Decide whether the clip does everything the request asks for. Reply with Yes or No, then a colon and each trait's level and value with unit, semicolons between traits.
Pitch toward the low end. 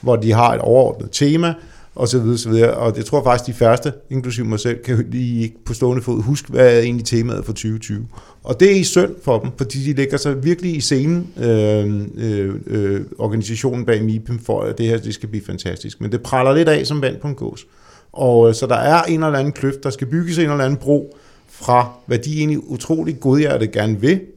Yes: low, 125 Hz